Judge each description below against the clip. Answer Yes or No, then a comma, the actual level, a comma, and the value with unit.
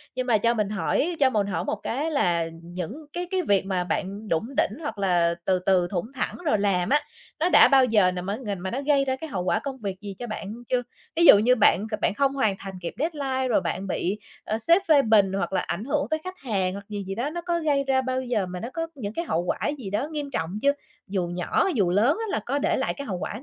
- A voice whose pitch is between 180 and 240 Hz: Yes, high, 220 Hz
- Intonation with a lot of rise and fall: Yes, wide, 6.4 semitones